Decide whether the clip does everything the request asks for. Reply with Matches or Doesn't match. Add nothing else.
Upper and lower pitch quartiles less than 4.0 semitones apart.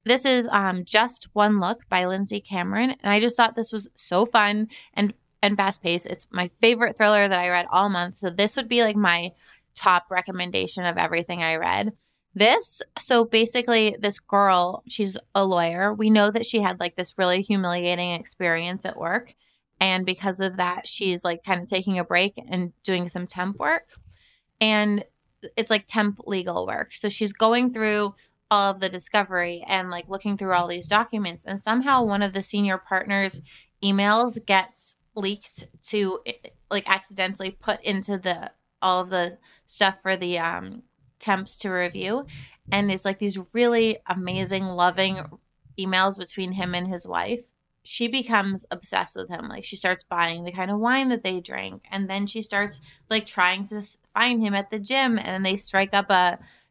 Matches